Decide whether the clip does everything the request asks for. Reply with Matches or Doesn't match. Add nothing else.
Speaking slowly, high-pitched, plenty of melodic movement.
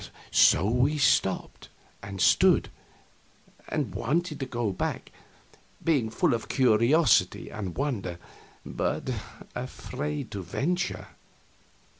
Doesn't match